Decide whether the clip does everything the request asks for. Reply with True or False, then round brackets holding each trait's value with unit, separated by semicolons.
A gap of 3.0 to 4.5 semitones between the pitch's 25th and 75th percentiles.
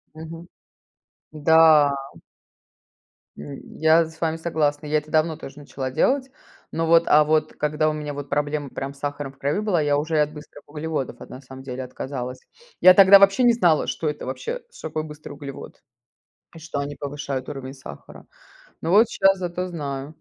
False (2.5 semitones)